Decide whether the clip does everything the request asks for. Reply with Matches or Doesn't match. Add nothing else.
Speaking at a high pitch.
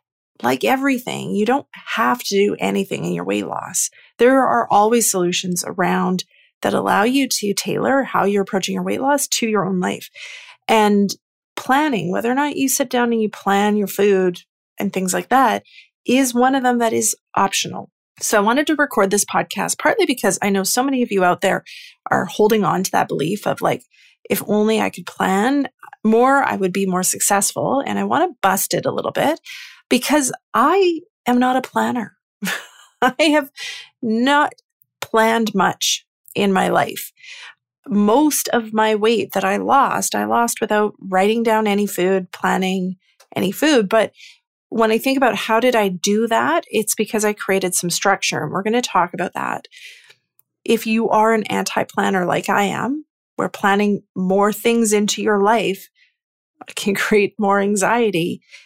Matches